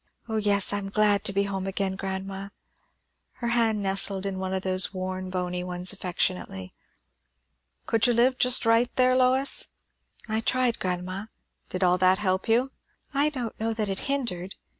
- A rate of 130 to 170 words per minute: Yes, average, 165 wpm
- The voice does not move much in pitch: No, average, 3.4 semitones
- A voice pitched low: No, high, 200 Hz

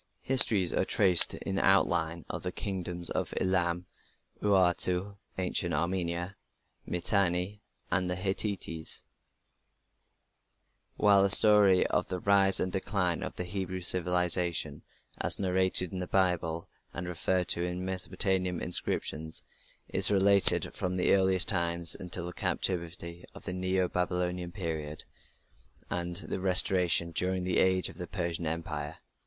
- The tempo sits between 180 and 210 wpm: No, slow, 135 wpm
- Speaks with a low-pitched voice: Yes, very low, 90 Hz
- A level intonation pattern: Yes, narrow, 1.6 semitones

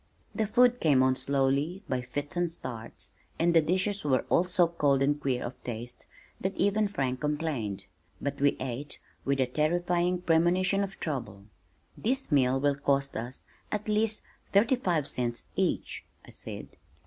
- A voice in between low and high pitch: Yes, medium, 150 Hz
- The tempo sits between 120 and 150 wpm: No, average, 160 wpm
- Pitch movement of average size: No, wide, 5.7 semitones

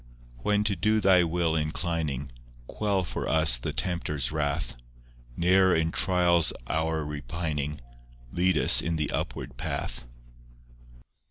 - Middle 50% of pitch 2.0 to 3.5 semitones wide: Yes, average, 3.1 semitones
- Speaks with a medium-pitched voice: No, very low, 80 Hz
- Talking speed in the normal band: No, slow, 125 wpm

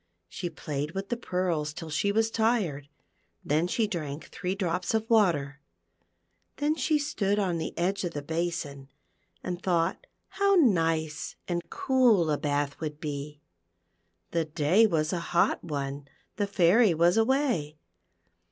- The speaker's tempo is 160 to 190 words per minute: No, average, 145 wpm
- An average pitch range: No, wide, 5.7 semitones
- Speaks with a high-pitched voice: No, medium, 175 Hz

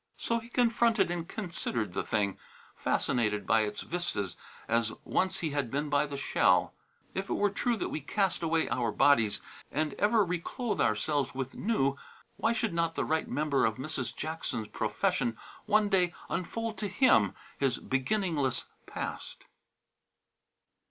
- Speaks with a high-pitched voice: No, medium, 155 Hz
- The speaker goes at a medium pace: Yes, average, 155 wpm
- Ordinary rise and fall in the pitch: No, wide, 8.3 semitones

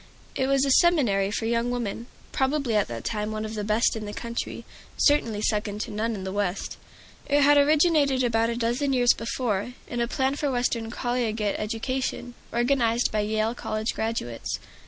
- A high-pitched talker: Yes, high, 235 Hz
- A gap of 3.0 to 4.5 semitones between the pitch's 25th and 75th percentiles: Yes, average, 3.4 semitones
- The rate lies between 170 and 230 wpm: Yes, average, 180 wpm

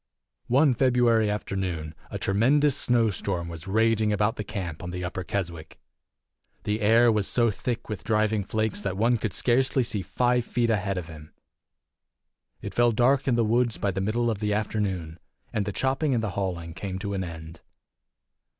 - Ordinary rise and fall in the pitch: Yes, average, 3.9 semitones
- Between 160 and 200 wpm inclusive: Yes, average, 180 wpm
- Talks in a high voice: No, low, 105 Hz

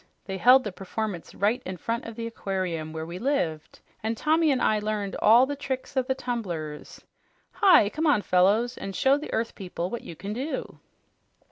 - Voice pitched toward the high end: Yes, high, 215 Hz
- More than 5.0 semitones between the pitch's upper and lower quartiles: Yes, wide, 5.6 semitones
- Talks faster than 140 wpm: Yes, average, 195 wpm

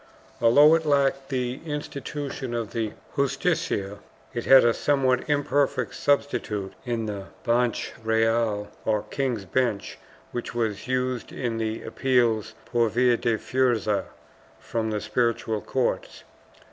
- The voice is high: No, low, 120 Hz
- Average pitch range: Yes, average, 3.3 semitones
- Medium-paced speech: No, slow, 125 wpm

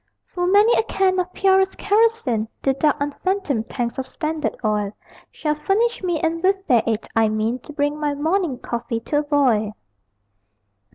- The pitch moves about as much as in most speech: No, wide, 7.7 semitones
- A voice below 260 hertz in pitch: No, very high, 300 Hz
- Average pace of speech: Yes, average, 170 wpm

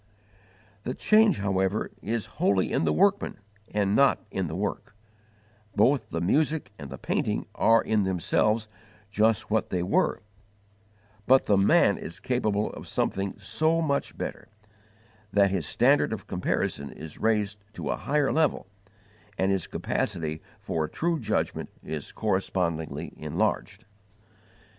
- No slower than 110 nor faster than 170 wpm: Yes, average, 140 wpm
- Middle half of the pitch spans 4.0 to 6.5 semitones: Yes, average, 5.1 semitones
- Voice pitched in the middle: No, low, 105 Hz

